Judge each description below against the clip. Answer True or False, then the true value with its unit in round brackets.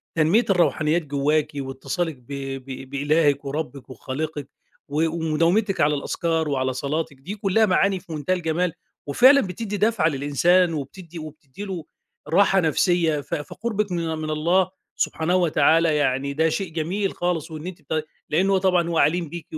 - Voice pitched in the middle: True (160 Hz)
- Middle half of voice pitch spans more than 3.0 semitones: True (3.7 semitones)